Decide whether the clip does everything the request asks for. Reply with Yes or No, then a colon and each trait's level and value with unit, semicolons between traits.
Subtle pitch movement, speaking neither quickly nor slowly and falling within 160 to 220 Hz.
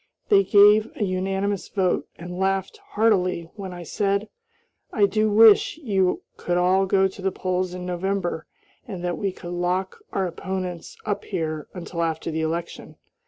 Yes: narrow, 2.2 semitones; average, 165 wpm; high, 190 Hz